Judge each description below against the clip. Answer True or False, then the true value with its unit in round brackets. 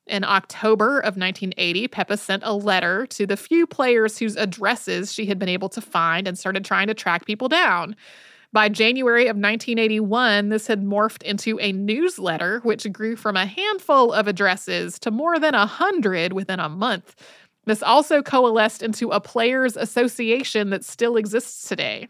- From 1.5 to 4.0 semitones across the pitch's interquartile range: True (2.9 semitones)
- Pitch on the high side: True (215 Hz)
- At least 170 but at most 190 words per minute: True (175 wpm)